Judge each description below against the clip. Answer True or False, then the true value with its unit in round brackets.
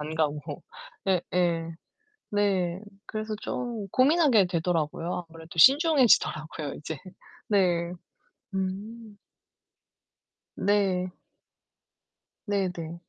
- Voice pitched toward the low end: False (185 Hz)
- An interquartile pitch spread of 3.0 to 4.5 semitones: True (4.0 semitones)